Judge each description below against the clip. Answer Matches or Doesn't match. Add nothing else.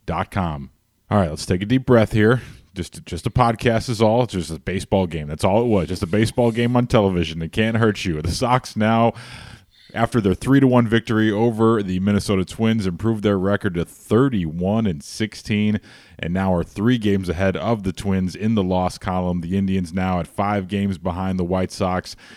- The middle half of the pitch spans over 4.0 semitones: Doesn't match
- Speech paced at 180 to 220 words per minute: Matches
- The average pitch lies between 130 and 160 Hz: Doesn't match